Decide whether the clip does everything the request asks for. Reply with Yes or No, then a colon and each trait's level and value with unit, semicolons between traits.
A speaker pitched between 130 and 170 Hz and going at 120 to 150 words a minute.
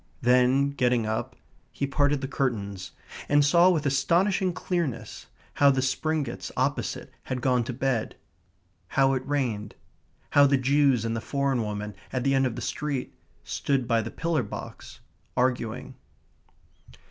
Yes: low, 135 Hz; average, 145 wpm